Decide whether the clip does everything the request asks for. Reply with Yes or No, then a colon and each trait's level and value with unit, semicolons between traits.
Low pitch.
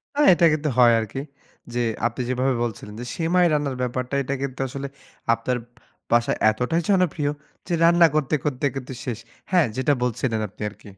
Yes: low, 130 Hz